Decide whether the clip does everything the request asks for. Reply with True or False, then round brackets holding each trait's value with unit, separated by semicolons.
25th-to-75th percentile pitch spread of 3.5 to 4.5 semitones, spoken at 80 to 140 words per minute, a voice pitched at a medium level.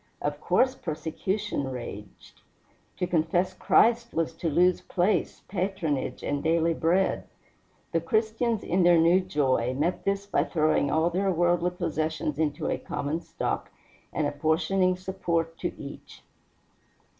False (3.1 semitones; 135 wpm; 170 Hz)